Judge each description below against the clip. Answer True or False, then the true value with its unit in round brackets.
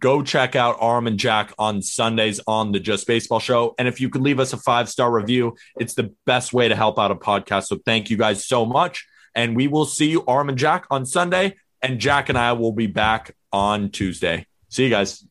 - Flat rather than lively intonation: False (3.1 semitones)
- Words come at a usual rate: False (235 wpm)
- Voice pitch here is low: True (120 Hz)